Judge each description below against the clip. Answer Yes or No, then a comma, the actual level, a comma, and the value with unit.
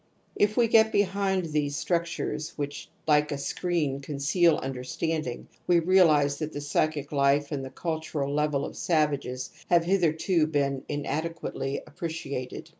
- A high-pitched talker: No, medium, 150 Hz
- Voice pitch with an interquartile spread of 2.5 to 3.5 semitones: Yes, average, 3.1 semitones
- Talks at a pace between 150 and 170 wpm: No, slow, 135 wpm